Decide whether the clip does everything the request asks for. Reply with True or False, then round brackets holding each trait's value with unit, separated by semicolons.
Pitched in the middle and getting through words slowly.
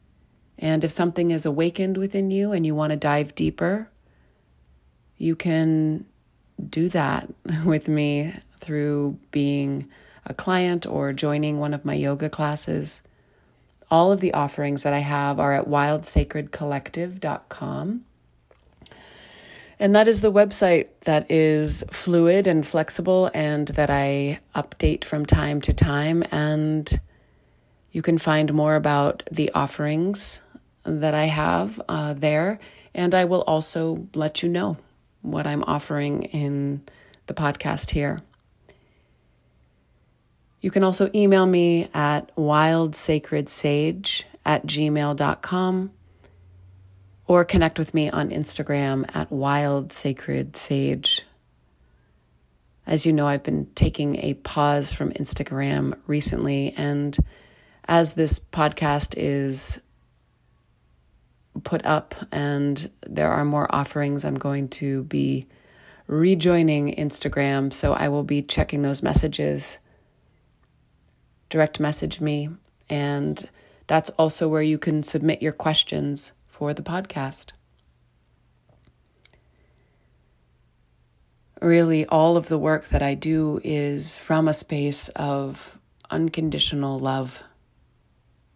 True (150 Hz; 115 wpm)